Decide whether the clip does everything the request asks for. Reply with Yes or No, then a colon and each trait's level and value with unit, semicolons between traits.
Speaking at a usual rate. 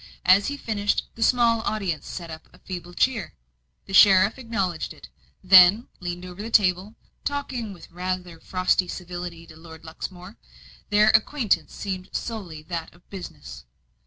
Yes: average, 150 wpm